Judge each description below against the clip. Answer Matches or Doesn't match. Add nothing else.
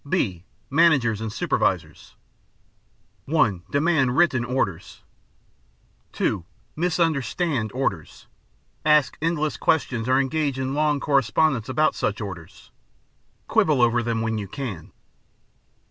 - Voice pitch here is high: Doesn't match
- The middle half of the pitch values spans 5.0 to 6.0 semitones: Matches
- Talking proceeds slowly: Matches